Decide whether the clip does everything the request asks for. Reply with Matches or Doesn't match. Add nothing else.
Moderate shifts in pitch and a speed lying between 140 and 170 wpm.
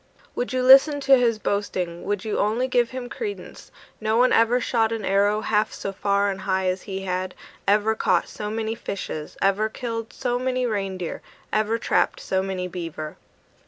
Doesn't match